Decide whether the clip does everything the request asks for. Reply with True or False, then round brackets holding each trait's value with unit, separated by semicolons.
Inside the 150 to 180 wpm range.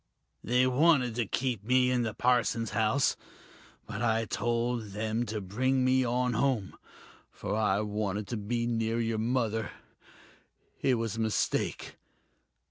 False (140 wpm)